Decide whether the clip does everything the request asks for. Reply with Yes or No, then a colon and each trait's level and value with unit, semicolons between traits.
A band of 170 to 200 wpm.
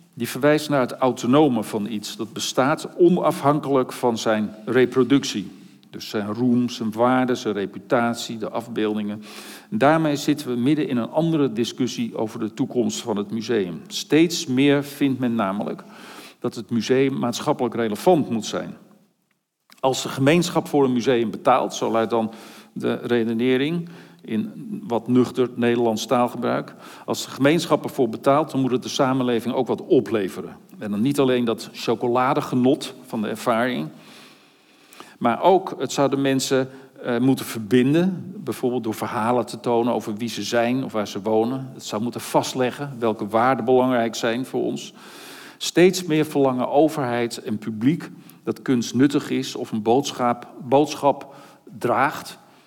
No: average, 155 wpm